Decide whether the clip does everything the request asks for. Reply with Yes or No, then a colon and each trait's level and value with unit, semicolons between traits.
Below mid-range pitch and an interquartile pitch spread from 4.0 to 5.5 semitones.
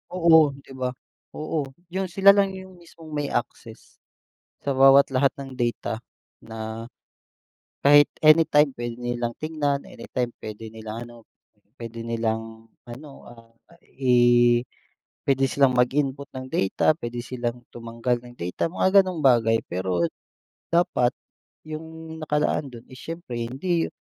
Yes: low, 130 Hz; average, 4.7 semitones